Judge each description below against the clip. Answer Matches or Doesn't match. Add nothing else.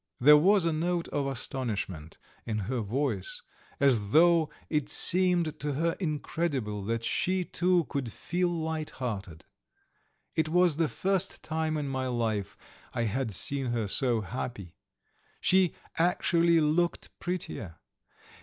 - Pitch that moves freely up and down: Matches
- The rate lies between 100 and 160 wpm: Matches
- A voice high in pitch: Doesn't match